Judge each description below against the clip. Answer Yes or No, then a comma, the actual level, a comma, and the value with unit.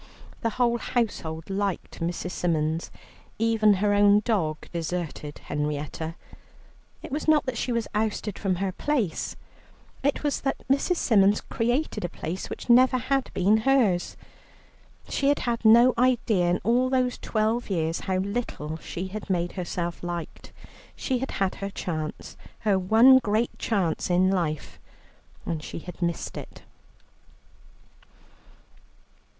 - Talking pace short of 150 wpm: Yes, average, 140 wpm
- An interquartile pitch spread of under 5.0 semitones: No, wide, 5.5 semitones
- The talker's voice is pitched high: Yes, high, 205 Hz